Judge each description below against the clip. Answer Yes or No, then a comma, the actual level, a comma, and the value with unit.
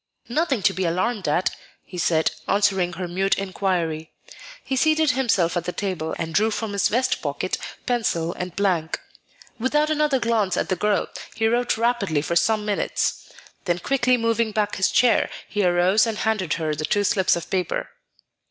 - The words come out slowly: No, average, 175 wpm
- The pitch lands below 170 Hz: No, high, 200 Hz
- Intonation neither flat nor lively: Yes, average, 4.8 semitones